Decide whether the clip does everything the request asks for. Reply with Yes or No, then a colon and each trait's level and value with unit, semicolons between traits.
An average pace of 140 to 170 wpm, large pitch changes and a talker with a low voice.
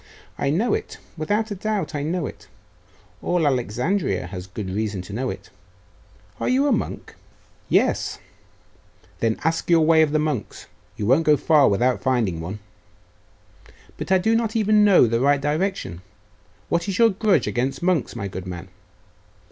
No: average, 165 wpm; wide, 9.0 semitones; medium, 150 Hz